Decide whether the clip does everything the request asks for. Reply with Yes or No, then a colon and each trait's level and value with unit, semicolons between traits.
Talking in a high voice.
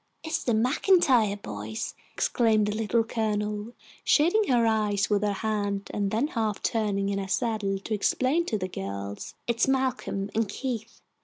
Yes: high, 215 Hz